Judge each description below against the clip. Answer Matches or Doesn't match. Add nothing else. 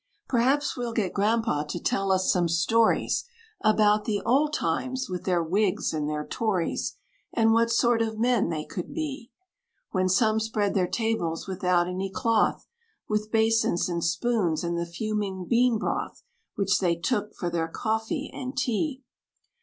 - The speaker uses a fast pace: Doesn't match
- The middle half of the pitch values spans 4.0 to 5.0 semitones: Matches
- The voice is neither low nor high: Doesn't match